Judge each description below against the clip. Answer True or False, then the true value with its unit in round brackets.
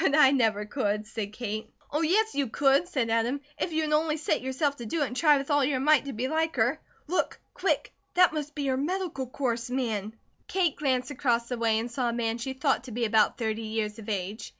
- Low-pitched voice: False (260 Hz)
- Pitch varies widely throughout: False (4.6 semitones)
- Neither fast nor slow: False (240 wpm)